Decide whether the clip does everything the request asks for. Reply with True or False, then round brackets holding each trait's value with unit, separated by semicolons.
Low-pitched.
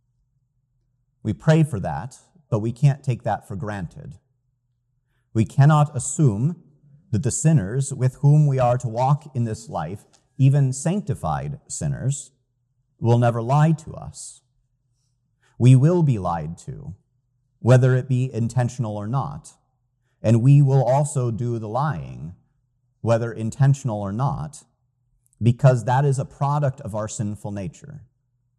True (130 Hz)